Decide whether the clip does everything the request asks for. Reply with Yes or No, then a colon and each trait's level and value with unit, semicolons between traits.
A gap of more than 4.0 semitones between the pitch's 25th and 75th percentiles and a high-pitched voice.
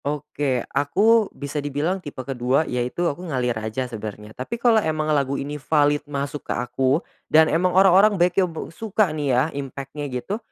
No: average, 4.7 semitones; medium, 145 Hz